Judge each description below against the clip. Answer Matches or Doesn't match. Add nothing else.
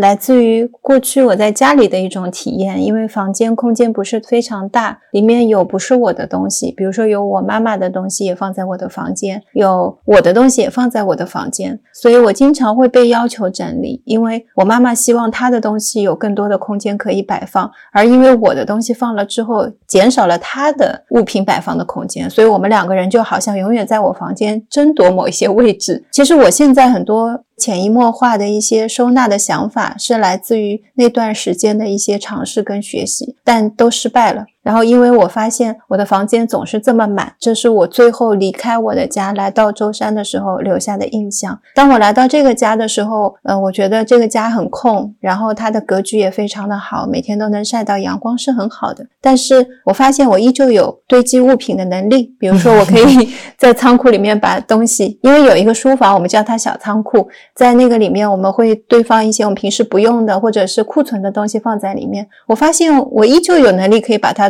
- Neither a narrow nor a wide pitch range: Matches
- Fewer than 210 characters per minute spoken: Doesn't match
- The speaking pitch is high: Matches